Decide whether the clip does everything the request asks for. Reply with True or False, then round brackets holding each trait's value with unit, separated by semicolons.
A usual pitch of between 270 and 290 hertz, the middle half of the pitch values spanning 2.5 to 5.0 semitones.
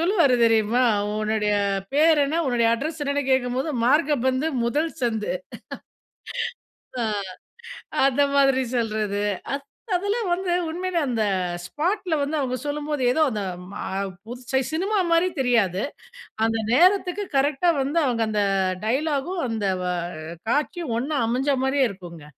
False (275 Hz; 5.5 semitones)